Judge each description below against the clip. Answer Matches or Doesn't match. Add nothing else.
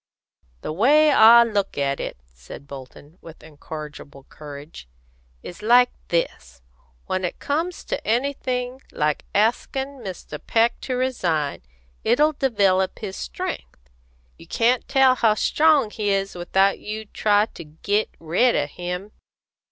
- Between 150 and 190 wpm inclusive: Doesn't match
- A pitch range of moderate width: Doesn't match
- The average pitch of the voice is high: Matches